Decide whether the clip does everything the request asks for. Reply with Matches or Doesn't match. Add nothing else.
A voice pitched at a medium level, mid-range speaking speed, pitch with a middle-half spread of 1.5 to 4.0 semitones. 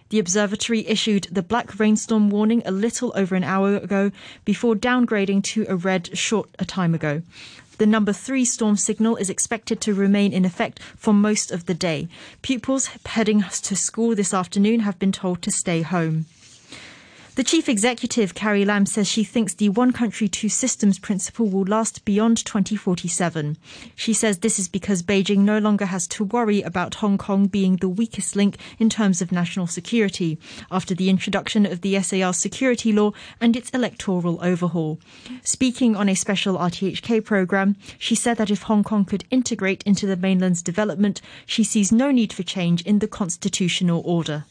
Doesn't match